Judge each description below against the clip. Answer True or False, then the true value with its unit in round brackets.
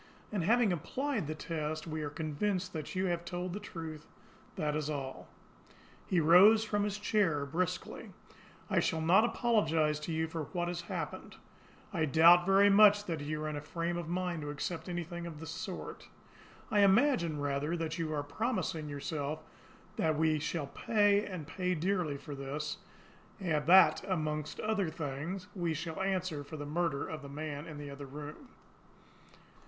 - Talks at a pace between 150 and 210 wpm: True (170 wpm)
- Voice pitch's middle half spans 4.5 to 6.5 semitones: False (3.6 semitones)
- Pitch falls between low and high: True (165 Hz)